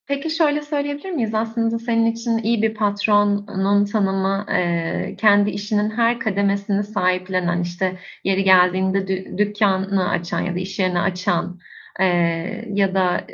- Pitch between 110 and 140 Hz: No, high, 200 Hz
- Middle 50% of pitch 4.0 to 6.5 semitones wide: No, average, 3.0 semitones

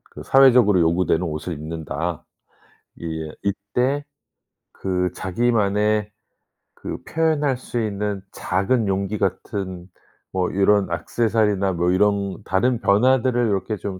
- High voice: No, low, 100 Hz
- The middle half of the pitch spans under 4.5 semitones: Yes, average, 3.8 semitones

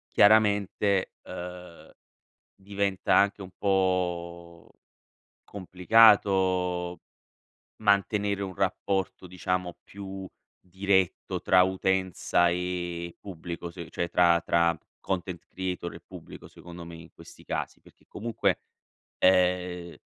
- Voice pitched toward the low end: Yes, very low, 90 Hz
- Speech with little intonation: Yes, narrow, 1.9 semitones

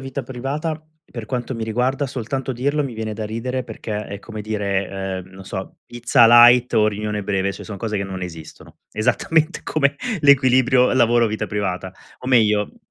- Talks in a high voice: No, low, 115 Hz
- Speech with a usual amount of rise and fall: Yes, average, 3.7 semitones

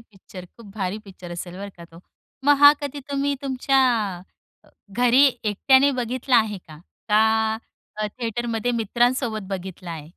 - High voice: Yes, high, 220 Hz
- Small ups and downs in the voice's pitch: No, average, 4.8 semitones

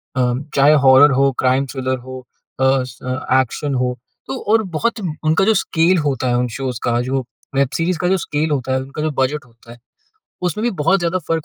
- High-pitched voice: No, low, 135 Hz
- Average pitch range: Yes, average, 3.8 semitones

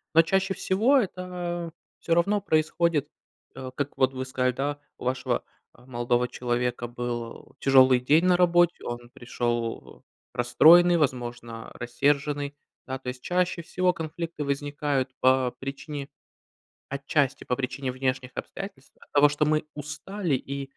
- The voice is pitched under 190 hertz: Yes, medium, 140 Hz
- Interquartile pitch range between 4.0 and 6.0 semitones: Yes, average, 4.7 semitones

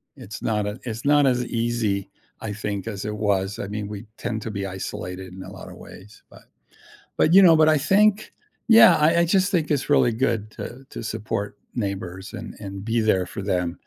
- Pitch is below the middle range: Yes, low, 110 Hz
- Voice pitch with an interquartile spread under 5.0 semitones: No, wide, 5.5 semitones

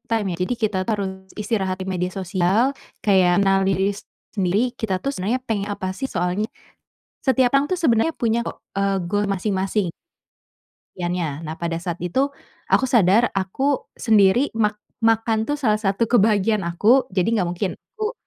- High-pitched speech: Yes, high, 205 Hz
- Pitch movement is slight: No, average, 3.6 semitones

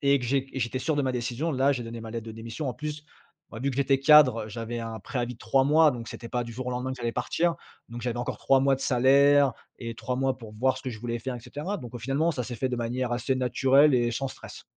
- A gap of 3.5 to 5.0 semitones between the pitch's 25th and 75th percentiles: No, narrow, 2.5 semitones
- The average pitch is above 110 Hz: Yes, low, 125 Hz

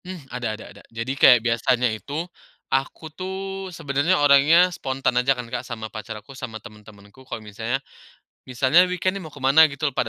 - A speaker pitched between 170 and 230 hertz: No, low, 135 Hz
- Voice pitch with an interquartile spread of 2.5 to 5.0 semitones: No, wide, 5.6 semitones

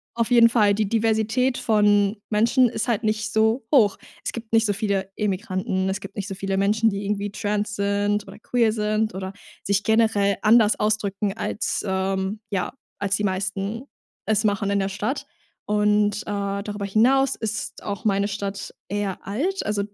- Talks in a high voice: Yes, high, 210 Hz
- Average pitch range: No, narrow, 1.8 semitones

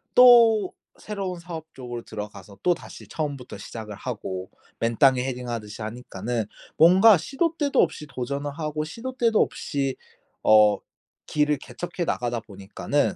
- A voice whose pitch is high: No, medium, 140 Hz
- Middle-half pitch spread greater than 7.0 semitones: Yes, wide, 7.4 semitones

